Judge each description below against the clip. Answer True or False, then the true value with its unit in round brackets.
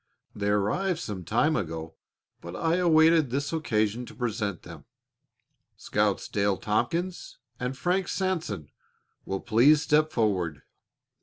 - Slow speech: True (125 wpm)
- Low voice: True (120 Hz)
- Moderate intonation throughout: False (8.1 semitones)